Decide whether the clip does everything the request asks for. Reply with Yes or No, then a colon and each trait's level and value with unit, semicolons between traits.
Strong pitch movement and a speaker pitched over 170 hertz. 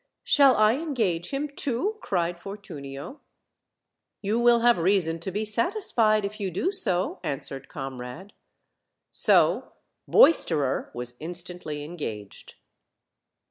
Yes: wide, 7.2 semitones; high, 190 Hz